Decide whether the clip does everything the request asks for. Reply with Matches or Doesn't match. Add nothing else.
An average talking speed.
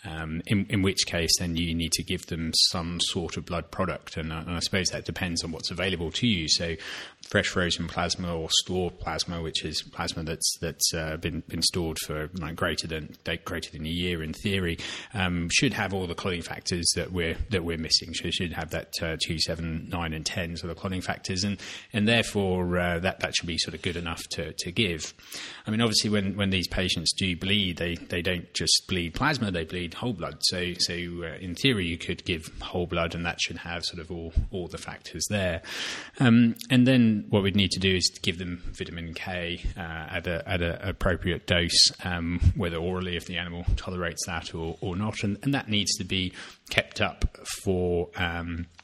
Doesn't match